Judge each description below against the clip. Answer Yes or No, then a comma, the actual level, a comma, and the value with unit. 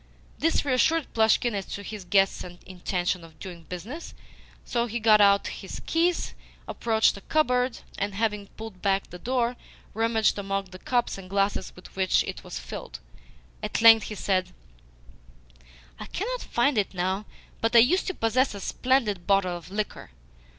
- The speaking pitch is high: Yes, high, 210 Hz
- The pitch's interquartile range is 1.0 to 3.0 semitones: No, average, 3.9 semitones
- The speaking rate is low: No, average, 165 wpm